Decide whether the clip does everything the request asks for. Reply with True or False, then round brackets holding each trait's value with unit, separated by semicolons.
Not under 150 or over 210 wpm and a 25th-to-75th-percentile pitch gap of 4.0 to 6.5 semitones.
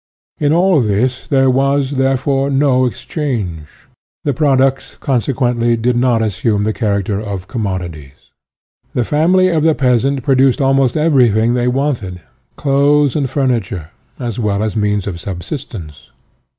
False (135 wpm; 4.8 semitones)